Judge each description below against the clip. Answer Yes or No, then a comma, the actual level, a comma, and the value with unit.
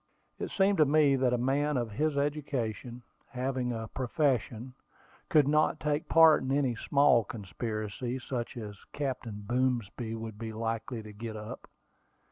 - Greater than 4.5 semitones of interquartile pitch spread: No, average, 4.0 semitones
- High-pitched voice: No, low, 125 Hz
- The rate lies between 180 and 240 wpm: No, average, 150 wpm